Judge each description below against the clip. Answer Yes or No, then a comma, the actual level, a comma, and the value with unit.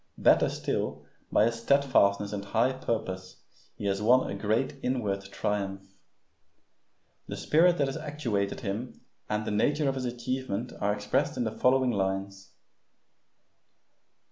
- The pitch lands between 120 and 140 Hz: No, low, 110 Hz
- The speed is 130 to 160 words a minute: Yes, average, 140 wpm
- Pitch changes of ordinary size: Yes, average, 4.7 semitones